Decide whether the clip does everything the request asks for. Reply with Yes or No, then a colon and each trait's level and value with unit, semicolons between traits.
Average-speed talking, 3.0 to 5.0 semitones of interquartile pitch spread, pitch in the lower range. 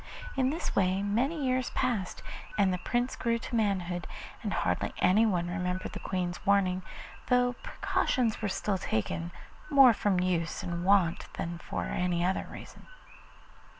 No: average, 150 wpm; average, 4.6 semitones; high, 195 Hz